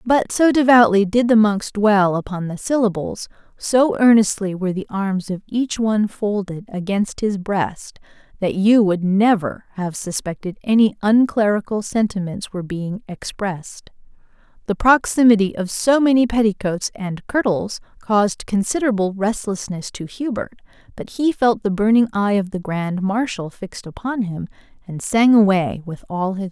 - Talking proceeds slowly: No, average, 150 wpm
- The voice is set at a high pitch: Yes, high, 205 Hz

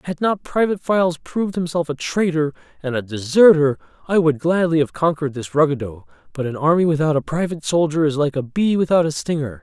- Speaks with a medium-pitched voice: Yes, medium, 155 Hz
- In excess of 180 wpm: Yes, average, 200 wpm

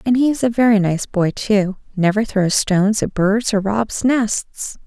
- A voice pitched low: No, high, 210 Hz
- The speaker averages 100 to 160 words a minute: No, average, 185 wpm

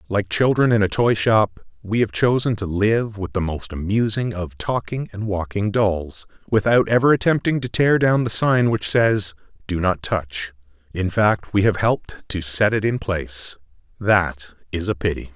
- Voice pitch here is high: No, low, 100 Hz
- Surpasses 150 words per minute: Yes, average, 185 wpm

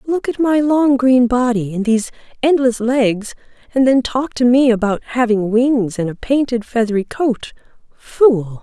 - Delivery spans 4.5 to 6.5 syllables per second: No, 4.3 syllables/s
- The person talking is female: Yes, female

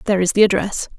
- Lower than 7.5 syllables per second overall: No, 7.8 syllables/s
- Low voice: No, high, 200 Hz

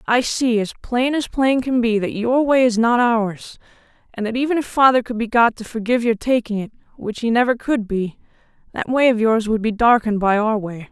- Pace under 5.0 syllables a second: No, 5.1 syllables/s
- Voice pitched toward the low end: No, high, 230 Hz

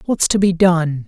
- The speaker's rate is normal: No, fast, 225 wpm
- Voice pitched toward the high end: No, medium, 175 Hz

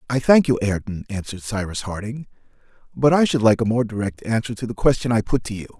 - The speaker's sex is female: No, male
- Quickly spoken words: Yes, fast, 230 wpm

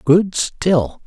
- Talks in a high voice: No, medium, 165 Hz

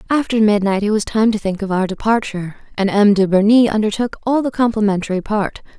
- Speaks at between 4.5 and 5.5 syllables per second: No, 6.0 syllables/s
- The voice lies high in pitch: Yes, high, 210 Hz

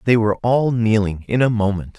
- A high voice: No, low, 110 Hz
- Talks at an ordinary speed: No, fast, 210 wpm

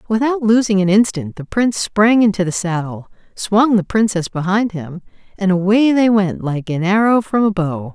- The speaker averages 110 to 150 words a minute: No, average, 190 wpm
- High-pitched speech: Yes, high, 200 Hz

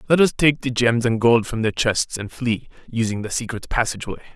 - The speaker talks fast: Yes, fast, 220 wpm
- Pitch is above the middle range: No, low, 120 Hz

